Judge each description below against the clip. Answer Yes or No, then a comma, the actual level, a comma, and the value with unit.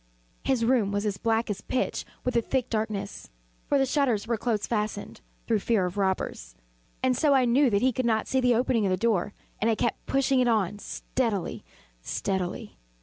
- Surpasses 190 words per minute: Yes, average, 200 wpm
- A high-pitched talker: Yes, high, 225 Hz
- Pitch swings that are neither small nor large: Yes, average, 3.8 semitones